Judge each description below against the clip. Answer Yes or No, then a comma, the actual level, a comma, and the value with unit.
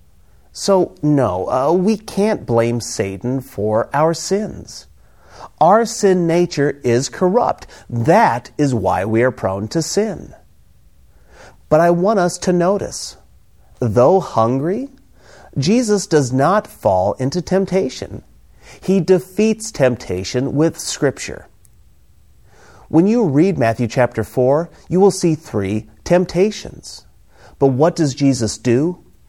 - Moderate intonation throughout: No, wide, 8.1 semitones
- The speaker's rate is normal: No, slow, 120 wpm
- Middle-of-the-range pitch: Yes, medium, 150 Hz